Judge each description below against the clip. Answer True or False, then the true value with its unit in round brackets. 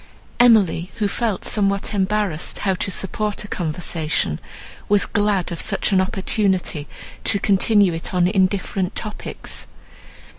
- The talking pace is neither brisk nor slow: False (125 wpm)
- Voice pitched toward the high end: True (195 Hz)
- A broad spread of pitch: False (2.5 semitones)